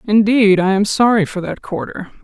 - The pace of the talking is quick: No, average, 190 wpm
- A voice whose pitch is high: Yes, high, 205 Hz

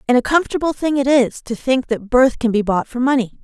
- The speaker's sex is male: No, female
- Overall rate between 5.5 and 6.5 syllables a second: Yes, 5.9 syllables/s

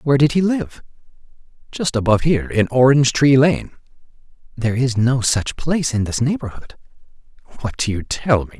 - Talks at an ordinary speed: Yes, average, 170 wpm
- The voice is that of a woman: No, male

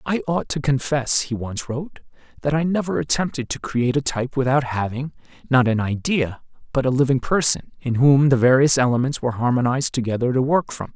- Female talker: No, male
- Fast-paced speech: No, average, 190 wpm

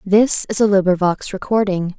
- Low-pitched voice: No, high, 195 Hz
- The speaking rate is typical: Yes, average, 150 wpm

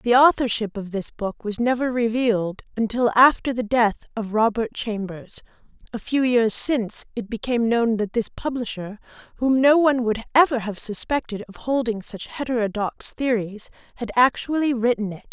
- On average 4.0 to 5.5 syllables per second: Yes, 5.1 syllables/s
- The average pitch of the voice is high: Yes, high, 230 Hz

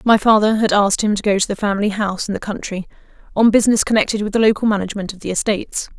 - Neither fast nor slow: No, fast, 240 wpm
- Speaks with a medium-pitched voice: No, high, 205 Hz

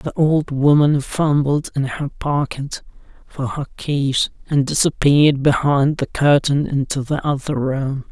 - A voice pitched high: No, medium, 140 Hz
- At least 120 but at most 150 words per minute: Yes, average, 140 wpm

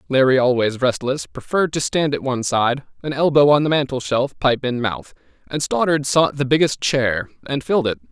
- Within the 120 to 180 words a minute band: No, average, 190 wpm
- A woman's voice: No, male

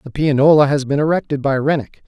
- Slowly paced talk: No, fast, 205 wpm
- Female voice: No, male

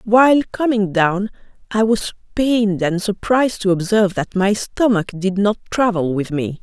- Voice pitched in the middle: No, high, 205 Hz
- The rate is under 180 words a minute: Yes, average, 165 wpm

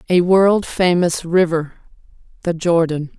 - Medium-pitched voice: Yes, medium, 175 Hz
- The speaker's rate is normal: No, slow, 95 wpm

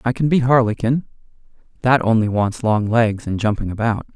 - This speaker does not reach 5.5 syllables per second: Yes, 5.3 syllables/s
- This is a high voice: No, low, 115 Hz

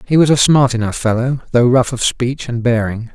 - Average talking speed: No, fast, 230 wpm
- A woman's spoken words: No, male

